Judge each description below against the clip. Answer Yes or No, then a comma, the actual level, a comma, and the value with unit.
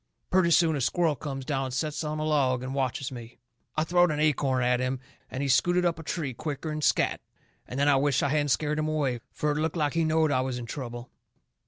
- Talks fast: Yes, fast, 240 wpm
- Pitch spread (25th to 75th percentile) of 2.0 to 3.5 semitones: Yes, average, 3.1 semitones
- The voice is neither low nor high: Yes, medium, 145 Hz